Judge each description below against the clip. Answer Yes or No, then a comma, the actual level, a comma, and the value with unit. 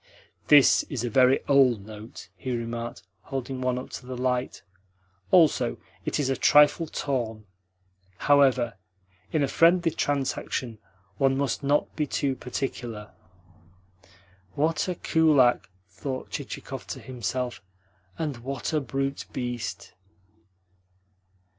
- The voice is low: Yes, low, 130 Hz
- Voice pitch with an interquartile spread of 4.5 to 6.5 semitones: No, average, 2.8 semitones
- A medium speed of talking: No, slow, 120 wpm